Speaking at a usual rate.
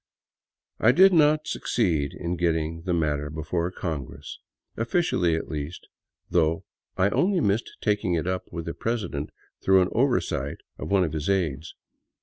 Yes: average, 160 wpm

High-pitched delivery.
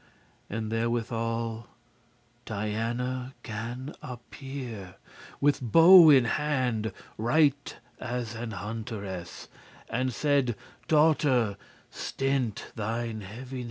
No: low, 120 Hz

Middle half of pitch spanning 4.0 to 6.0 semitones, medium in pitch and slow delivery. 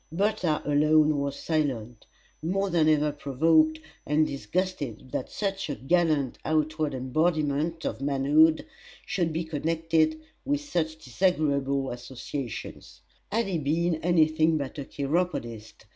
No: average, 2.9 semitones; medium, 155 Hz; slow, 125 wpm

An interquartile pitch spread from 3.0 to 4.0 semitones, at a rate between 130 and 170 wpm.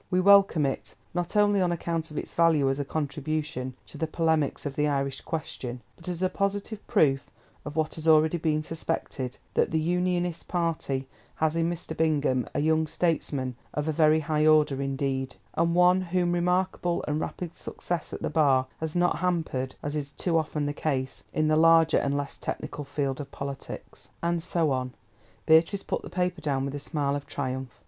No: average, 3.3 semitones; average, 190 wpm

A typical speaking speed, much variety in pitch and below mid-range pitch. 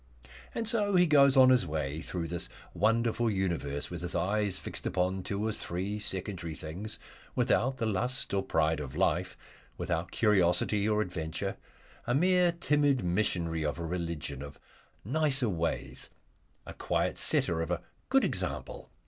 Yes: average, 155 wpm; wide, 6.5 semitones; very low, 95 Hz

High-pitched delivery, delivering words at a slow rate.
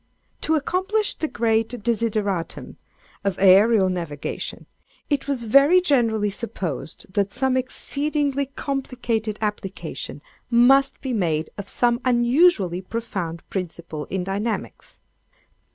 Yes: high, 225 Hz; slow, 105 wpm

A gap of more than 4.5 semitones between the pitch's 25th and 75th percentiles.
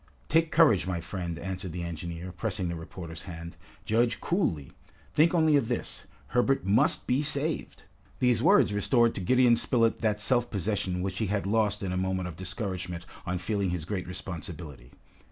Yes: average, 5.0 semitones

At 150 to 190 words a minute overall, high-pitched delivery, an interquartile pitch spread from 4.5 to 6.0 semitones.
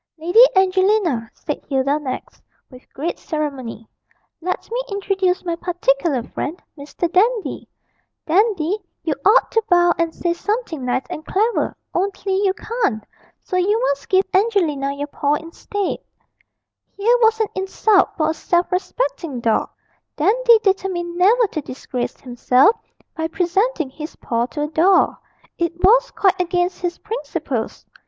No: average, 140 wpm; very high, 350 Hz; average, 5.3 semitones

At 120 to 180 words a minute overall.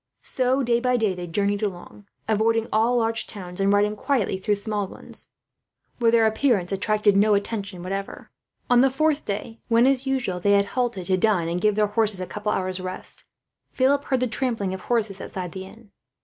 No: average, 200 wpm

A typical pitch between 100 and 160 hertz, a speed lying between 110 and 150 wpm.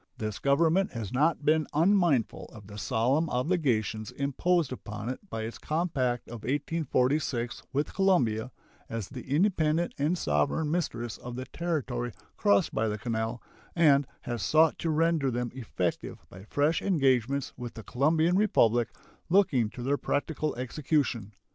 Yes: low, 135 Hz; average, 145 wpm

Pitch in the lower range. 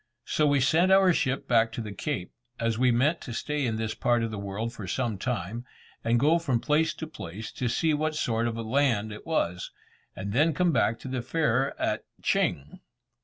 Yes: low, 120 Hz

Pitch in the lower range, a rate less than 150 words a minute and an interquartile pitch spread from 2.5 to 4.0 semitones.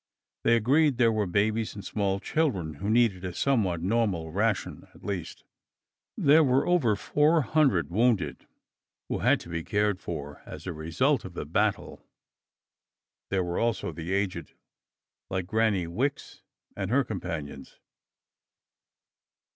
No: low, 100 Hz; average, 140 wpm; average, 5.1 semitones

